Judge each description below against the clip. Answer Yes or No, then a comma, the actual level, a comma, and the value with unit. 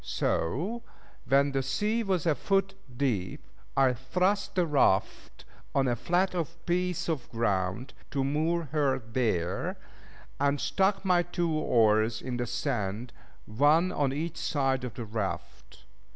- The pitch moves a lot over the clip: Yes, wide, 6.3 semitones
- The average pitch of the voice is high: No, medium, 140 Hz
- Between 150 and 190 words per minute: No, slow, 135 wpm